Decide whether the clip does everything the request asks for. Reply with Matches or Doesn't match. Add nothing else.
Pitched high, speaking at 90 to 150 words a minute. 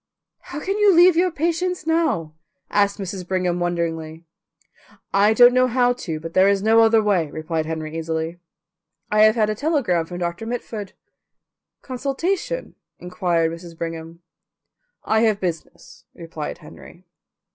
Matches